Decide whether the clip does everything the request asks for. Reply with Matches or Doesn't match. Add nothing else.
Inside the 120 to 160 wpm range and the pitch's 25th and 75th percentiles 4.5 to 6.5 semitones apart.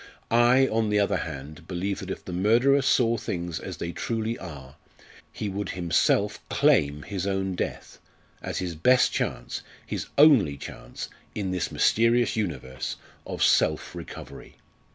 Matches